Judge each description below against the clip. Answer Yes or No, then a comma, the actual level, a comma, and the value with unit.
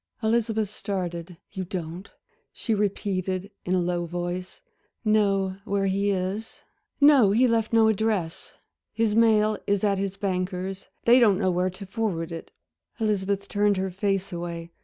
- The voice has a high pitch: Yes, high, 195 Hz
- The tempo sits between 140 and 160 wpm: Yes, average, 150 wpm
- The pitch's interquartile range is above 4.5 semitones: No, average, 2.7 semitones